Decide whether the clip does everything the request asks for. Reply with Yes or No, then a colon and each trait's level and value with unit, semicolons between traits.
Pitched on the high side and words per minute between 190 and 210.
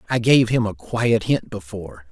No: low, 110 Hz; average, 200 wpm